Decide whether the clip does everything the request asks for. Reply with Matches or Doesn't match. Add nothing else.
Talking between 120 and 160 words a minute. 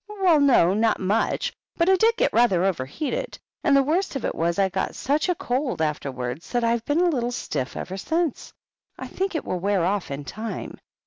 Doesn't match